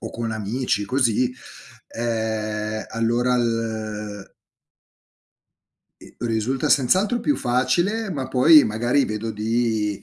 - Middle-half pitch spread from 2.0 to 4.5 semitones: Yes, average, 2.9 semitones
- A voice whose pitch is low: Yes, low, 115 Hz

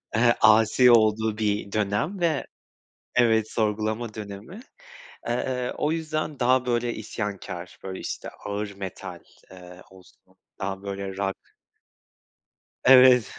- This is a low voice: Yes, low, 110 Hz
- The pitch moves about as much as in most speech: Yes, average, 3.8 semitones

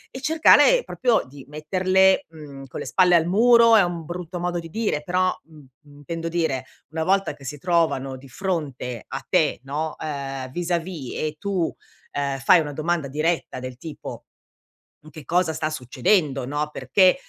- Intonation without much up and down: No, average, 4.4 semitones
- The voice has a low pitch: No, medium, 160 Hz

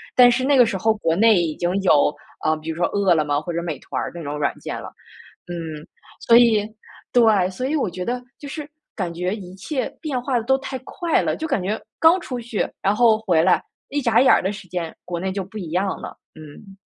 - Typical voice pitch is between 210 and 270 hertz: No, high, 195 Hz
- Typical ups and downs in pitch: No, wide, 6.0 semitones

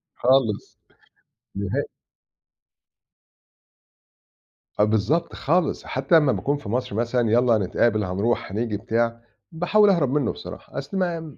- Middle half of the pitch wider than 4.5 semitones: Yes, average, 5.3 semitones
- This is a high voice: No, low, 125 Hz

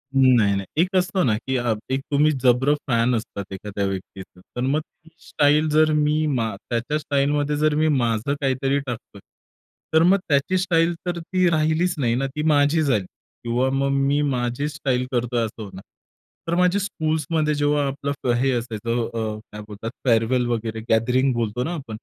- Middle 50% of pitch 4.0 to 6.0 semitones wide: Yes, average, 4.6 semitones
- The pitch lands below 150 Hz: Yes, low, 135 Hz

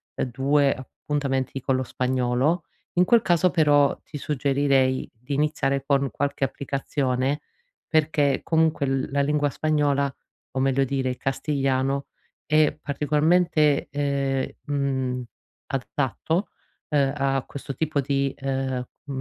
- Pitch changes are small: Yes, narrow, 1.8 semitones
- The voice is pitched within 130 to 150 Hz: Yes, medium, 140 Hz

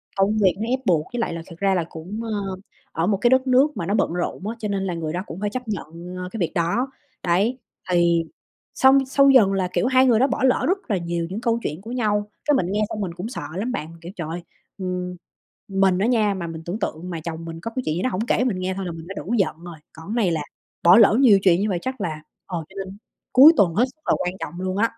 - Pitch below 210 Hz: Yes, high, 195 Hz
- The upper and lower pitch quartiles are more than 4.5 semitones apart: Yes, average, 5.0 semitones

